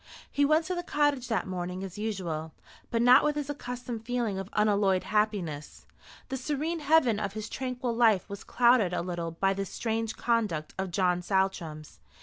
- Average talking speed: Yes, average, 175 wpm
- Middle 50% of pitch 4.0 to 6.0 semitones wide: Yes, average, 5.1 semitones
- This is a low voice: No, high, 215 Hz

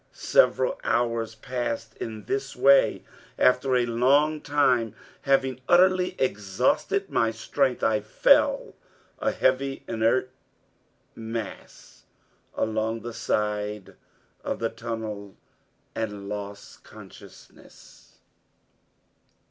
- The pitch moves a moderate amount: Yes, average, 3.5 semitones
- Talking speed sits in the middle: No, slow, 90 wpm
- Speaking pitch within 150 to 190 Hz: No, low, 115 Hz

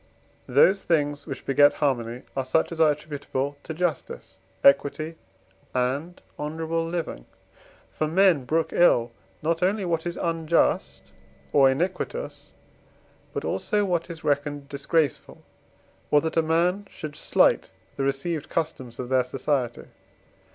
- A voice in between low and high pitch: Yes, medium, 155 Hz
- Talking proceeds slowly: Yes, slow, 130 wpm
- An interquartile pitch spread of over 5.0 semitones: No, average, 3.3 semitones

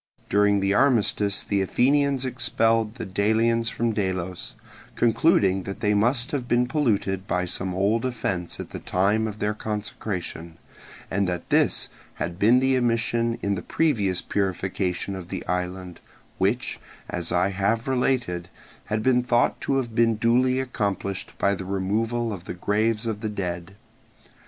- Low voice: Yes, low, 105 Hz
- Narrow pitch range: No, average, 3.8 semitones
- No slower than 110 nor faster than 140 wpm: No, average, 155 wpm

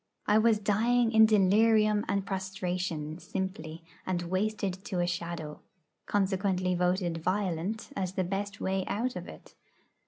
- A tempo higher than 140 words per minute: No, slow, 135 wpm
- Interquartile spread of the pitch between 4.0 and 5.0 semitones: No, average, 2.7 semitones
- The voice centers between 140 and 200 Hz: Yes, high, 190 Hz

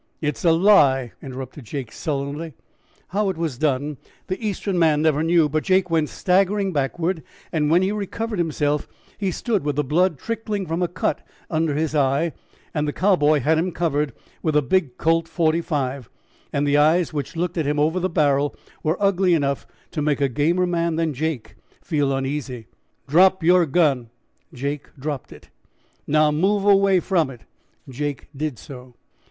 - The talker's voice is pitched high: No, medium, 155 Hz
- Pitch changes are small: No, average, 3.7 semitones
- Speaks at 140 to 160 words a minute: No, average, 170 wpm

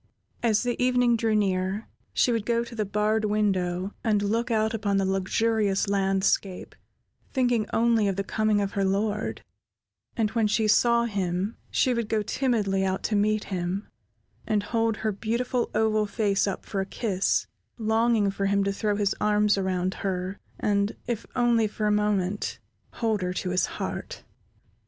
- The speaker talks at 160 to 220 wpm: Yes, average, 170 wpm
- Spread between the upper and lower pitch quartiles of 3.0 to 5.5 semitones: No, narrow, 2.4 semitones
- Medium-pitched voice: No, high, 210 Hz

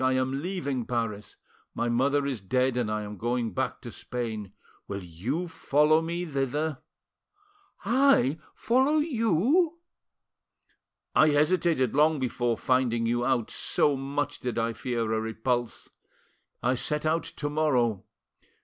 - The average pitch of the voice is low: Yes, low, 130 Hz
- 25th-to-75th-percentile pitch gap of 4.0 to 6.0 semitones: Yes, average, 4.7 semitones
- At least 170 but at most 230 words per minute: No, slow, 135 wpm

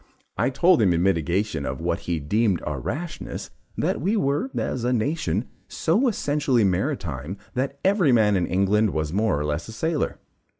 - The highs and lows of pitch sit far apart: Yes, wide, 8.5 semitones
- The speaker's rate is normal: Yes, average, 175 wpm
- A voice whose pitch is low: Yes, low, 110 Hz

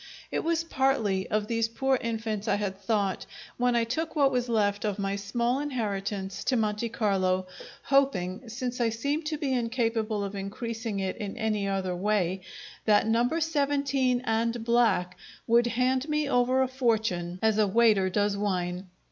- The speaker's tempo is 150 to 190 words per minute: Yes, average, 165 wpm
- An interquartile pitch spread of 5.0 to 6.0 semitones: No, average, 4.0 semitones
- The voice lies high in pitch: Yes, high, 225 Hz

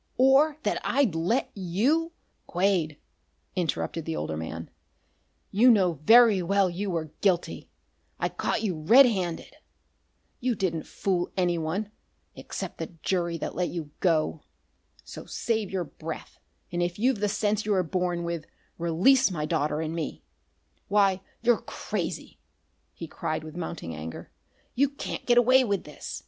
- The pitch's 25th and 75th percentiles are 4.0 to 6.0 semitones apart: Yes, average, 4.7 semitones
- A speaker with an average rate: Yes, average, 150 wpm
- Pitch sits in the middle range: Yes, medium, 180 Hz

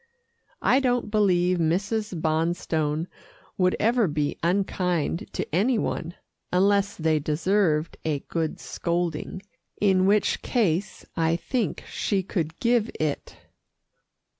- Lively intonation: No, average, 4.1 semitones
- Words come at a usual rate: No, slow, 115 wpm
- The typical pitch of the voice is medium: Yes, medium, 180 Hz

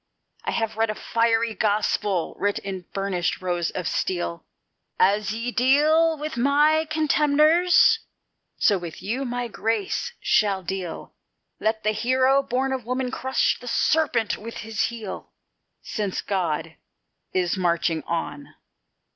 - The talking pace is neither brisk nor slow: No, slow, 130 wpm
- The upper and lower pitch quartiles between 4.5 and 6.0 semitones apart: Yes, wide, 5.5 semitones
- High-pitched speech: Yes, high, 225 Hz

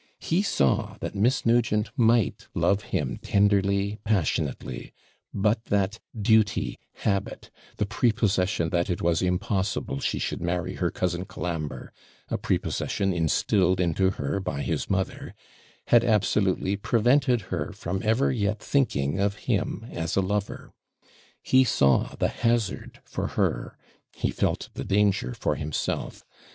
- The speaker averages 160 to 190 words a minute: No, slow, 135 wpm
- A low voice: Yes, low, 100 Hz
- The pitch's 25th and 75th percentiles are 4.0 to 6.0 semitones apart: No, average, 3.5 semitones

